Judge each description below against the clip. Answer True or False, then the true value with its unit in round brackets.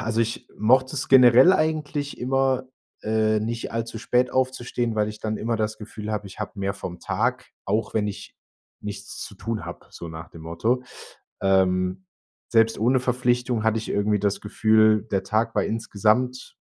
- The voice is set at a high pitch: False (110 Hz)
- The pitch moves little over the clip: False (3.0 semitones)